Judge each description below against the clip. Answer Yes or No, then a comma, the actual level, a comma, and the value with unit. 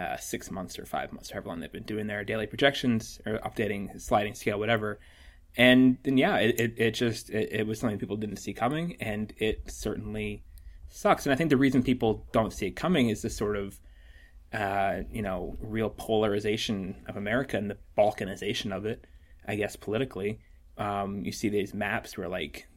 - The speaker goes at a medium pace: Yes, average, 195 wpm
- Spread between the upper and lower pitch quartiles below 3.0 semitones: Yes, narrow, 2.4 semitones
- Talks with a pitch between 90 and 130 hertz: Yes, low, 105 Hz